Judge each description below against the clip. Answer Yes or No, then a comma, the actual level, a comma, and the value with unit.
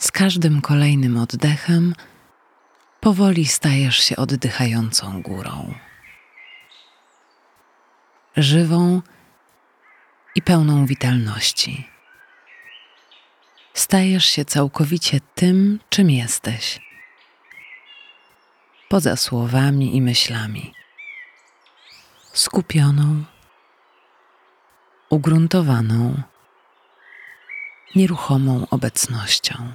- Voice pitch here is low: No, medium, 145 Hz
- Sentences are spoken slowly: Yes, slow, 55 wpm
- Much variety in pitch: Yes, wide, 5.9 semitones